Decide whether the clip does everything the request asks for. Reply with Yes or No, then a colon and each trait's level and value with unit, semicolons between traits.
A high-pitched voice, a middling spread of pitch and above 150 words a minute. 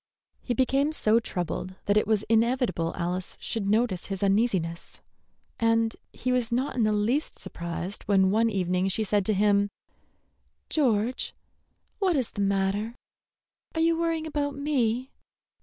No: high, 220 Hz; average, 4.5 semitones; average, 145 wpm